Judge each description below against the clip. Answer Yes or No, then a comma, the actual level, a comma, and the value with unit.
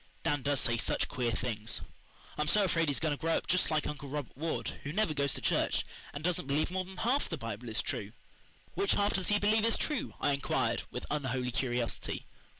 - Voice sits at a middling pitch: Yes, medium, 150 Hz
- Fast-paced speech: Yes, fast, 220 wpm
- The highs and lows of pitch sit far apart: Yes, wide, 6.2 semitones